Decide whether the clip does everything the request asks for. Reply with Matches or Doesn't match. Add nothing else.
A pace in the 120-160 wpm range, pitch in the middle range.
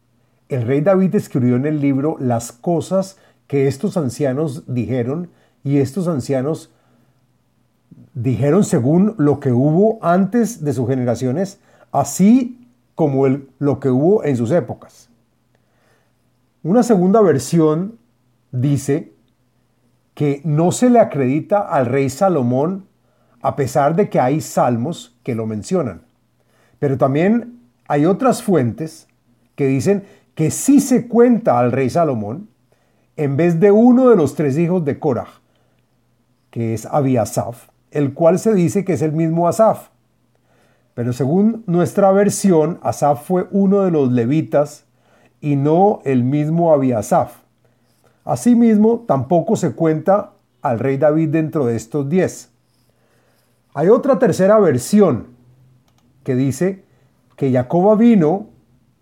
Matches